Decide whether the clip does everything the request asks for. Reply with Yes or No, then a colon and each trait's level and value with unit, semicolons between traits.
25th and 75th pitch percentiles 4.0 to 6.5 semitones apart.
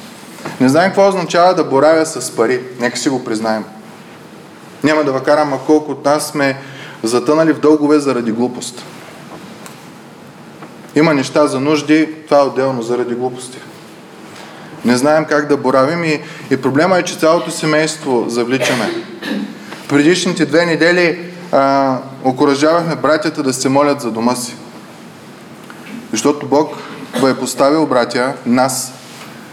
No: average, 3.4 semitones